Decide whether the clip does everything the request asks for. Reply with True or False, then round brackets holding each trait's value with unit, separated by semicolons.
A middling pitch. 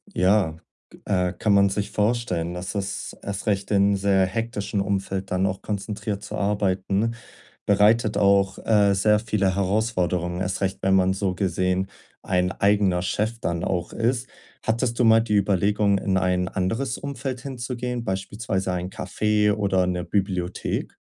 False (100 Hz)